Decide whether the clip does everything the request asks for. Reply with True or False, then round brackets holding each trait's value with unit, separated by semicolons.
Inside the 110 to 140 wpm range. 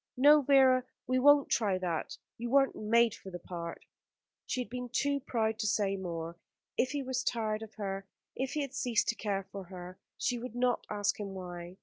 False (205 wpm)